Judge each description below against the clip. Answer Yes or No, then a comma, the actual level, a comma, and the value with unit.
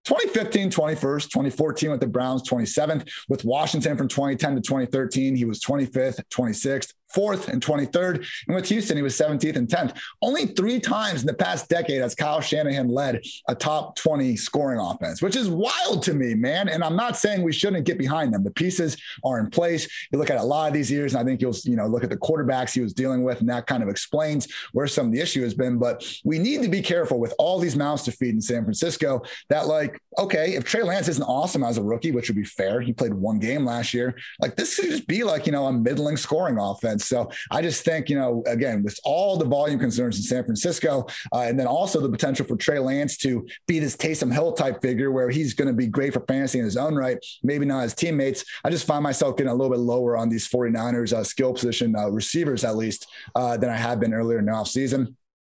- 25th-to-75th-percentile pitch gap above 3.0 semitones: Yes, average, 4.3 semitones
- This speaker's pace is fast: Yes, fast, 240 wpm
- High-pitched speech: No, low, 135 Hz